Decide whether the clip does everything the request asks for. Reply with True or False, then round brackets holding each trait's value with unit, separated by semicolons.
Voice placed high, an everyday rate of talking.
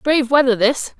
True (260 Hz; 180 wpm)